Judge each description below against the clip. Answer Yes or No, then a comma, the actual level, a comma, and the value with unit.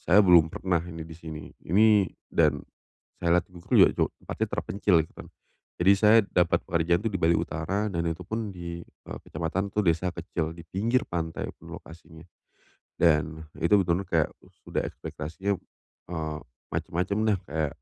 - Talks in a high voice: No, very low, 85 Hz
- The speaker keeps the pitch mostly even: No, average, 3.2 semitones